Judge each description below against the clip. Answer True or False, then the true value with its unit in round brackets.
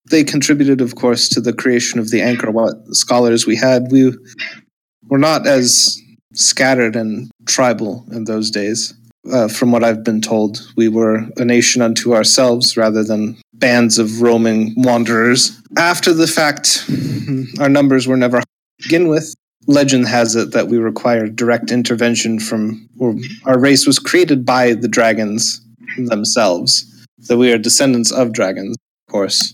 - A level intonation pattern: True (2.2 semitones)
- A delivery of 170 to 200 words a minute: False (160 wpm)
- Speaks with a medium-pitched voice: False (120 Hz)